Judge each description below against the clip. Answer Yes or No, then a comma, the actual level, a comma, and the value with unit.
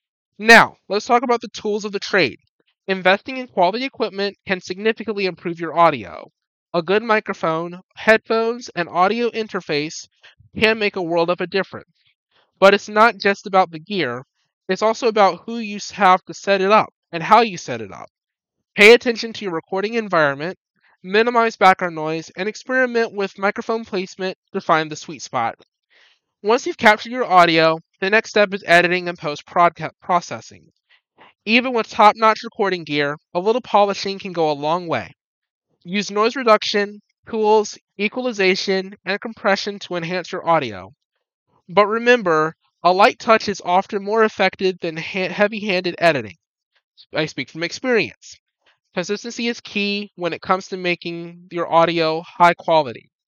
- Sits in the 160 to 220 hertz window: Yes, high, 190 Hz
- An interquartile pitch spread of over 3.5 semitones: Yes, average, 4.1 semitones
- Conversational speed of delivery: Yes, average, 160 wpm